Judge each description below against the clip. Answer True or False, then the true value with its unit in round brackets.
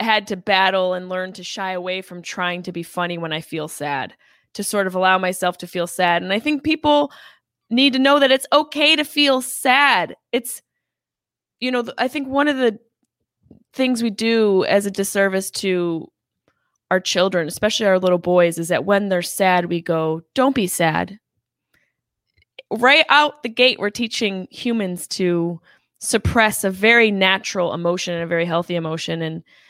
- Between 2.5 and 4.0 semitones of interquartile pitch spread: False (5.2 semitones)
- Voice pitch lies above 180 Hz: True (190 Hz)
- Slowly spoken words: False (180 wpm)